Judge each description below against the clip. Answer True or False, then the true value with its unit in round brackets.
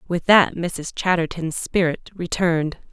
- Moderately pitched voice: True (170 Hz)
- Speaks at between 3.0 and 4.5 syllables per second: True (4.3 syllables/s)